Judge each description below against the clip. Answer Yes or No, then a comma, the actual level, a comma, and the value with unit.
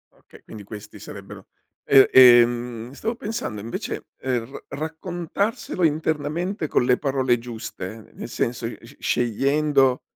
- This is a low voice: Yes, low, 130 Hz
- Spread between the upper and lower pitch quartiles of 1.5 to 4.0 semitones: No, average, 4.7 semitones